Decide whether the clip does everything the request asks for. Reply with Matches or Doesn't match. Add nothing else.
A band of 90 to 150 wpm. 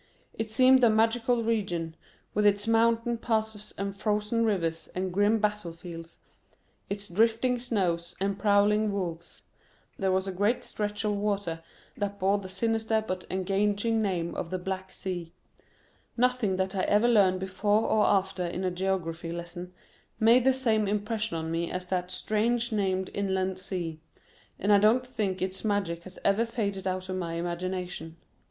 Doesn't match